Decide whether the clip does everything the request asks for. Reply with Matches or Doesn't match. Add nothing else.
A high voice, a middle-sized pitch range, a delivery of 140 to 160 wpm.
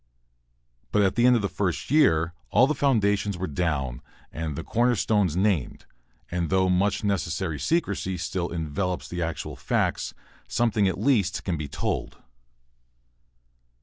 Doesn't match